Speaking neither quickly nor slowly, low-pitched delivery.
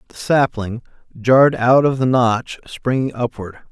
Yes: average, 145 wpm; low, 120 Hz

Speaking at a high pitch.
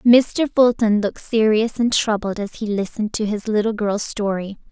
Yes: high, 215 Hz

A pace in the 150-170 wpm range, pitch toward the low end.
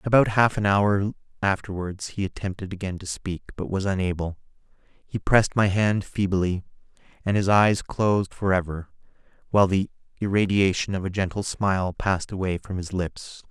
Yes: average, 155 wpm; very low, 95 Hz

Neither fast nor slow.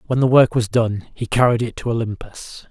No: fast, 220 wpm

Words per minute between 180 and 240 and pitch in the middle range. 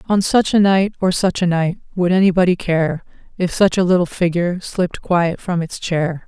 Yes: average, 200 wpm; medium, 180 Hz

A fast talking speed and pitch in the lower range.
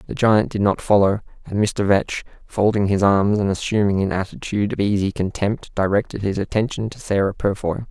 No: average, 180 wpm; low, 100 Hz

